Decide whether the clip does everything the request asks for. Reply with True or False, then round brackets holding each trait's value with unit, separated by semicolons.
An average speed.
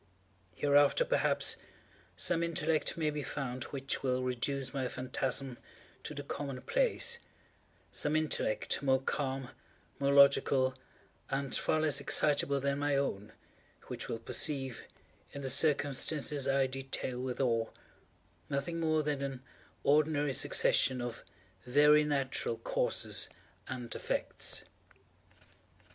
False (115 wpm)